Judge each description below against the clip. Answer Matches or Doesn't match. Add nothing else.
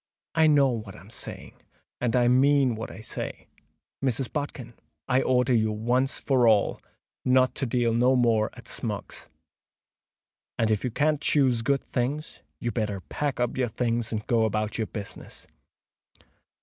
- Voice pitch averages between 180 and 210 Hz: Doesn't match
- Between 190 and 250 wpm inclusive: Doesn't match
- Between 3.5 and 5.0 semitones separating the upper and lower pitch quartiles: Doesn't match